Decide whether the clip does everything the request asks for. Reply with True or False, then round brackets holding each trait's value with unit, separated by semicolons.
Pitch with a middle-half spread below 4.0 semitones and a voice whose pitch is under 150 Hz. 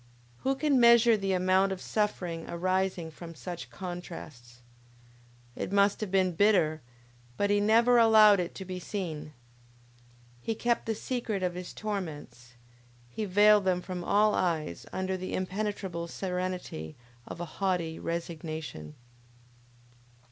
False (3.5 semitones; 185 Hz)